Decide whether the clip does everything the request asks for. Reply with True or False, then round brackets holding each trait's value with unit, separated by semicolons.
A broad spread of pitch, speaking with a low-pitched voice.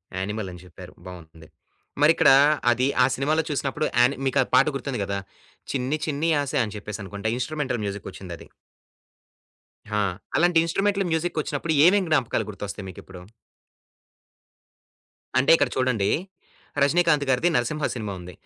True (7.3 semitones; 130 Hz)